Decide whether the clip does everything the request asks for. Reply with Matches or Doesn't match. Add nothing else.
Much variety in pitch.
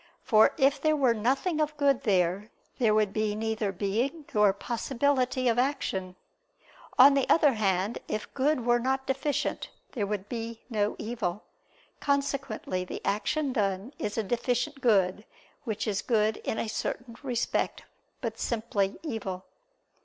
Doesn't match